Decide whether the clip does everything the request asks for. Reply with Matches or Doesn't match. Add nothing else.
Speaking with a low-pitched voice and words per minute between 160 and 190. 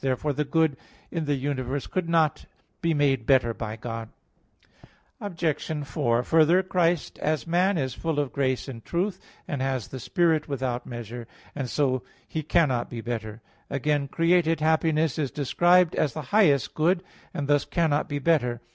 Doesn't match